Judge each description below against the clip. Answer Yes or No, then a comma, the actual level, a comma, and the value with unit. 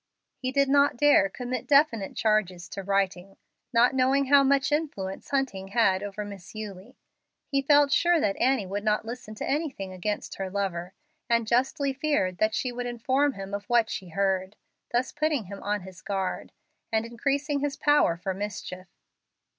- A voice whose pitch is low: No, high, 225 Hz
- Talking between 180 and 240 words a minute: No, average, 170 wpm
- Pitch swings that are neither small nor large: No, wide, 5.8 semitones